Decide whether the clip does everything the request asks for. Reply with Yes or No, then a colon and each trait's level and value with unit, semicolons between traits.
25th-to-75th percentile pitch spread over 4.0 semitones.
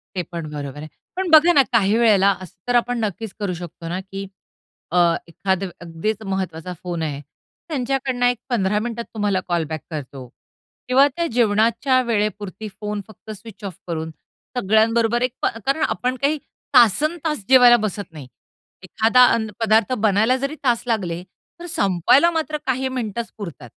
Yes: average, 5.1 semitones